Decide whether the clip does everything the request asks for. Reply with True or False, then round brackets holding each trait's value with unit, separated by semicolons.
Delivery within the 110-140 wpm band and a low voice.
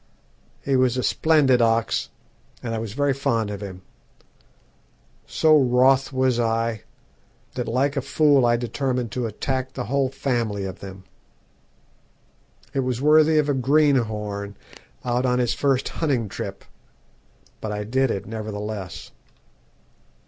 True (135 wpm; 125 Hz)